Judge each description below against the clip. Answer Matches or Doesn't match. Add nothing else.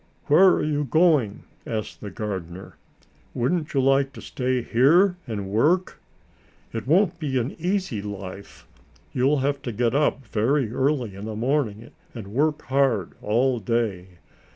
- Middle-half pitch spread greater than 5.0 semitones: Matches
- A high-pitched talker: Doesn't match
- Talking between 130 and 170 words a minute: Matches